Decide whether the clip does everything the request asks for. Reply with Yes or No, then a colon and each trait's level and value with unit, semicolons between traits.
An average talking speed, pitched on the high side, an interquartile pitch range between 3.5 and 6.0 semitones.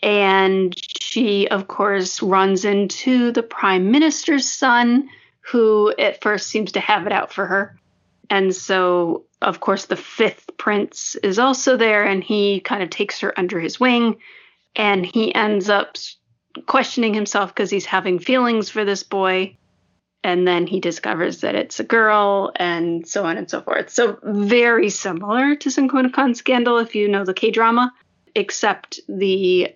Yes: average, 160 wpm; high, 205 Hz; average, 3.8 semitones